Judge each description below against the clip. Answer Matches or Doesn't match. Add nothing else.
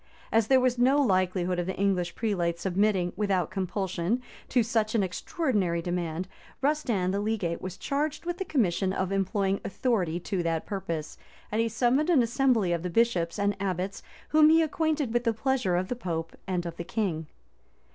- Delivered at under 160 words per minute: Doesn't match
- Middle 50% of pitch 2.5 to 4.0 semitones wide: Doesn't match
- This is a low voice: Doesn't match